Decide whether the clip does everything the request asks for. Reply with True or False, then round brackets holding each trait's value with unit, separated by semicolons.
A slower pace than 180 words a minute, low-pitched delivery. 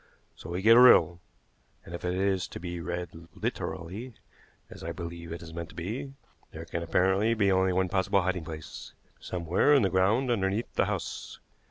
False (190 wpm; 95 Hz)